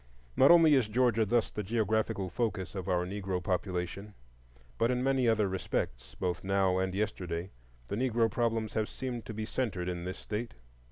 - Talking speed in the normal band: Yes, average, 175 wpm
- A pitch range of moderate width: Yes, average, 3.9 semitones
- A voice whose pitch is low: Yes, low, 105 Hz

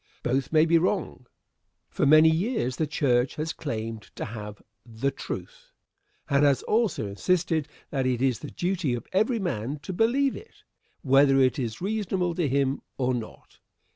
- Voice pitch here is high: No, medium, 145 Hz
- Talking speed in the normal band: Yes, average, 165 wpm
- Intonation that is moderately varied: No, wide, 6.1 semitones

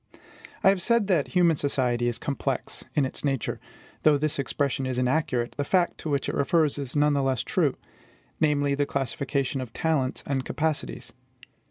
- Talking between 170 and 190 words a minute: Yes, average, 175 wpm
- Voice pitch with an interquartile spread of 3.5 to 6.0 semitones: No, average, 2.8 semitones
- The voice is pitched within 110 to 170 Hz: Yes, medium, 140 Hz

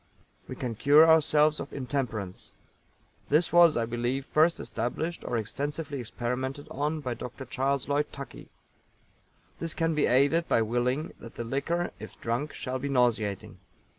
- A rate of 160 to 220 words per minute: No, average, 150 wpm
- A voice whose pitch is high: No, low, 135 Hz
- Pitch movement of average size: Yes, average, 4.0 semitones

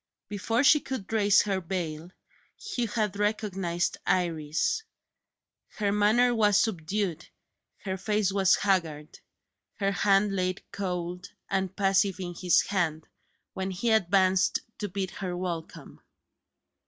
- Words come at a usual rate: No, slow, 120 wpm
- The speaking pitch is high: Yes, high, 195 Hz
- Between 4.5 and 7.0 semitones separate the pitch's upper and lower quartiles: No, average, 2.7 semitones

